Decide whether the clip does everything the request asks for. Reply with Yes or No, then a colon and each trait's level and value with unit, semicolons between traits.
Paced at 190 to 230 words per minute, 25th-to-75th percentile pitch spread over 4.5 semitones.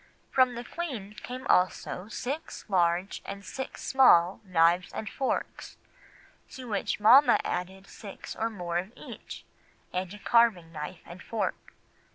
No: slow, 135 wpm; average, 4.9 semitones